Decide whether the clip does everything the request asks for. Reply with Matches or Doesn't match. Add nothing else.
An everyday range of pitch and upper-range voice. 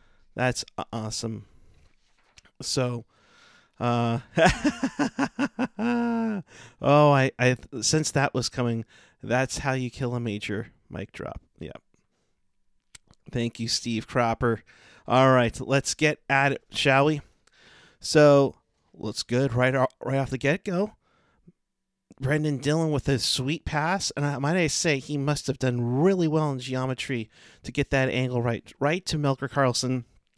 Doesn't match